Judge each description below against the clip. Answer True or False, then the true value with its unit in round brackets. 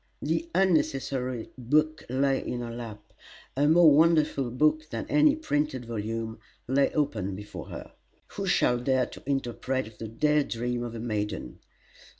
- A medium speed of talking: True (150 wpm)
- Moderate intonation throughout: True (4.6 semitones)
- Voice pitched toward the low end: True (130 Hz)